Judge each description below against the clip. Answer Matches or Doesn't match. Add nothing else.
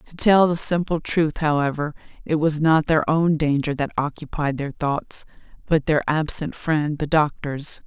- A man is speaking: Doesn't match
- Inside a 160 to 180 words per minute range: Matches